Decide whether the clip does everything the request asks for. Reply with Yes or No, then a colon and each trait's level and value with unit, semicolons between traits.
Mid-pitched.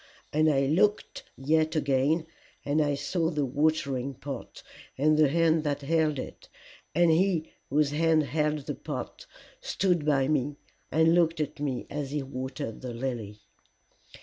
Yes: medium, 150 Hz